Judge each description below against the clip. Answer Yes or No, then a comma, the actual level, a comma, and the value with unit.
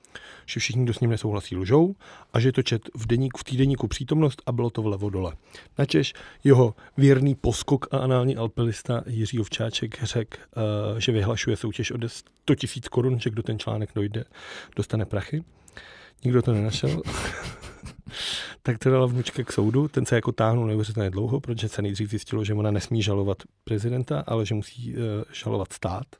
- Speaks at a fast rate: Yes, fast, 175 wpm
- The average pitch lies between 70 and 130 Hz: Yes, low, 115 Hz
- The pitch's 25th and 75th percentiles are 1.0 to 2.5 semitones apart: No, average, 2.9 semitones